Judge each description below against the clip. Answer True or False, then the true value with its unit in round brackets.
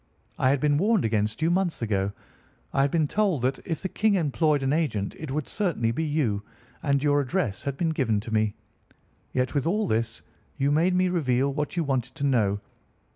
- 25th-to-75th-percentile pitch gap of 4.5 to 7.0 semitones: True (5.1 semitones)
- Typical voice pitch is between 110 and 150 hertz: True (140 Hz)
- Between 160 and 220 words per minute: True (200 wpm)